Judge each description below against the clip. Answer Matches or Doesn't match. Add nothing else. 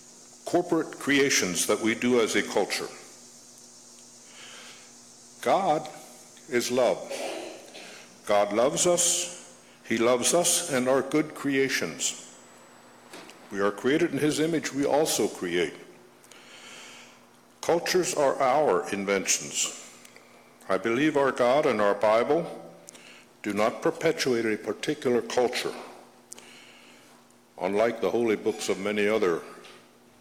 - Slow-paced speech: Matches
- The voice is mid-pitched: Doesn't match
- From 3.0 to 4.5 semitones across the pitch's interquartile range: Doesn't match